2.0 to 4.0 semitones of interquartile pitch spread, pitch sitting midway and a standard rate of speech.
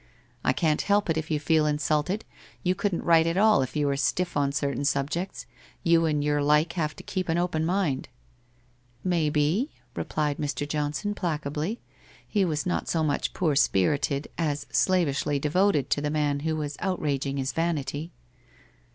Yes: average, 3.1 semitones; medium, 150 Hz; average, 175 wpm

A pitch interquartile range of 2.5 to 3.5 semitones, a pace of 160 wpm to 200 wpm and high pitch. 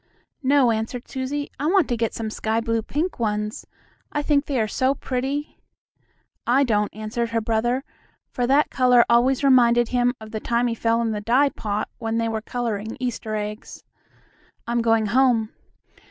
Yes: average, 2.8 semitones; average, 175 wpm; high, 235 Hz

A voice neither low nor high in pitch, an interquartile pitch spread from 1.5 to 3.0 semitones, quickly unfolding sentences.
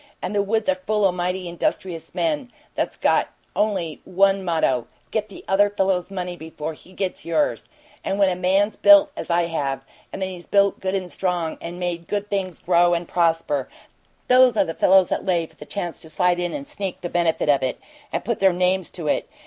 Yes: medium, 180 Hz; narrow, 2.6 semitones; fast, 210 wpm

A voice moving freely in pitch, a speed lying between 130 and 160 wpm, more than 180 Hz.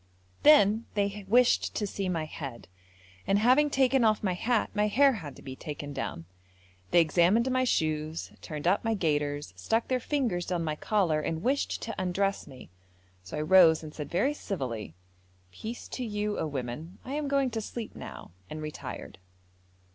No: wide, 7.1 semitones; average, 180 wpm; high, 190 Hz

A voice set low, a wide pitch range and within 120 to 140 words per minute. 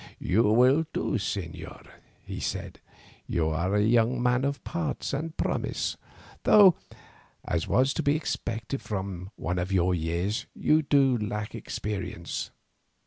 Yes: low, 110 Hz; wide, 6.7 semitones; slow, 135 wpm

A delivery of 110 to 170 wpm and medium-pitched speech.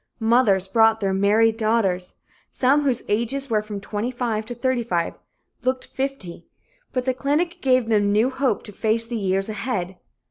No: average, 155 wpm; high, 225 Hz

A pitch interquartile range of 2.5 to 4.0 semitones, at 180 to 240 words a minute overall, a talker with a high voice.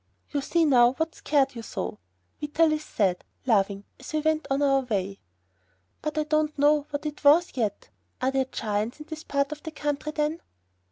Yes: average, 3.7 semitones; average, 185 wpm; very high, 290 Hz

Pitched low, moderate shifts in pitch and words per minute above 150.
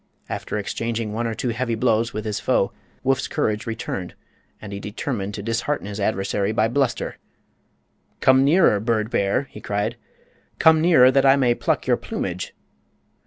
Yes: low, 115 Hz; average, 3.6 semitones; average, 165 wpm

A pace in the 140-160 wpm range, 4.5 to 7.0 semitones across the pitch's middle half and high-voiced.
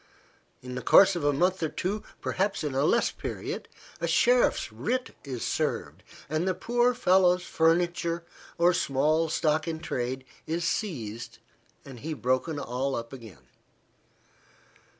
No: average, 145 wpm; average, 5.3 semitones; medium, 160 Hz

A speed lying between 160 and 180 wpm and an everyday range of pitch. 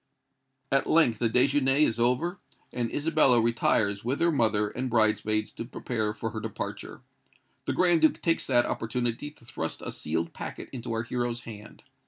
Yes: average, 170 wpm; average, 3.6 semitones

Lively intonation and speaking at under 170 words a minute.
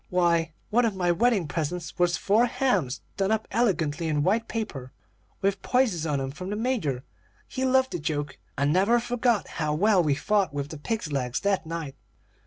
No: wide, 6.4 semitones; average, 190 wpm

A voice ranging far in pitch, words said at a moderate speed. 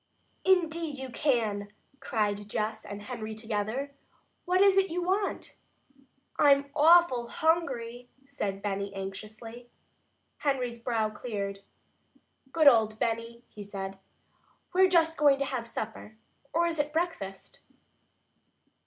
No: wide, 6.4 semitones; slow, 120 wpm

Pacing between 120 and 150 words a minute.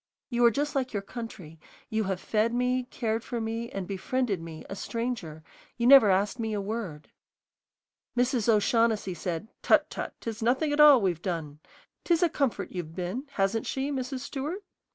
No: average, 175 wpm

